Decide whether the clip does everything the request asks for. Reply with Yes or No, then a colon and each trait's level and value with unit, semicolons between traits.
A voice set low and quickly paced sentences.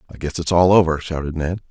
Yes: very low, 85 Hz; fast, 245 wpm